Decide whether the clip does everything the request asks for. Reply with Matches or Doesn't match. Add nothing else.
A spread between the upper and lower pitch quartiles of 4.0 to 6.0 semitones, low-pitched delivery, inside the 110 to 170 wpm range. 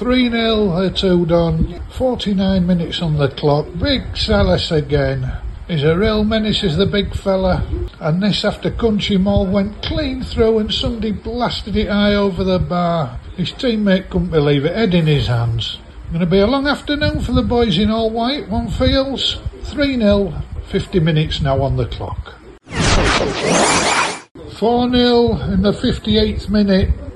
Doesn't match